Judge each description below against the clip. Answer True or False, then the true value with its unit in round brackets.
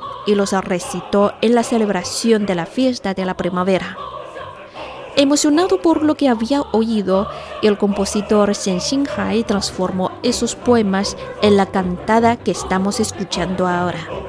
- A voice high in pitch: True (205 Hz)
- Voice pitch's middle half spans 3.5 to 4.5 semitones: True (3.8 semitones)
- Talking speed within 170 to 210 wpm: False (135 wpm)